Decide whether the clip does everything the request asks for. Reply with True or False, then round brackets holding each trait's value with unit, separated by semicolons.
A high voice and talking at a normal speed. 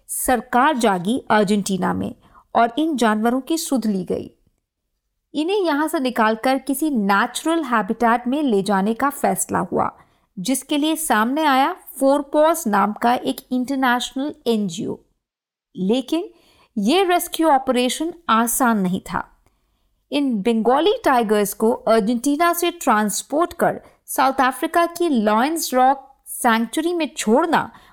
True (260 Hz; 125 wpm)